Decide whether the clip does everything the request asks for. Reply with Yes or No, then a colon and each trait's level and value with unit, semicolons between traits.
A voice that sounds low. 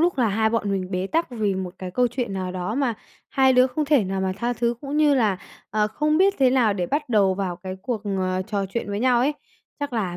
No: high, 220 Hz